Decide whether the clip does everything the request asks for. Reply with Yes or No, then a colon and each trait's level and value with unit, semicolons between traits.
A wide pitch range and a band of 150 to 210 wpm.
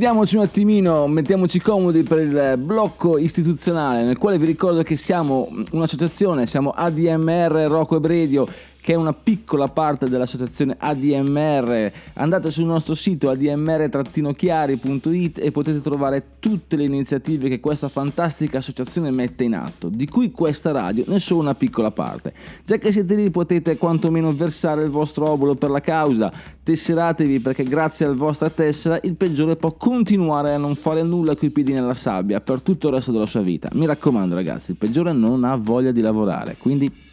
No: average, 3.4 semitones; fast, 170 wpm